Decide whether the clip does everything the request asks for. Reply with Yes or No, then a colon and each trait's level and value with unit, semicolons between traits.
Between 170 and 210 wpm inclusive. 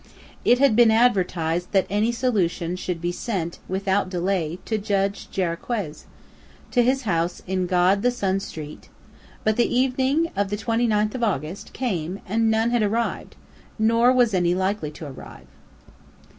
No: average, 155 wpm